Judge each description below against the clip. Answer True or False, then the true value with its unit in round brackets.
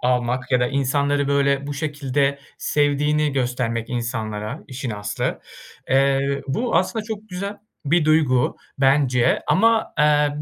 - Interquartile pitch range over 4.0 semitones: False (3.0 semitones)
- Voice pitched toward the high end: False (140 Hz)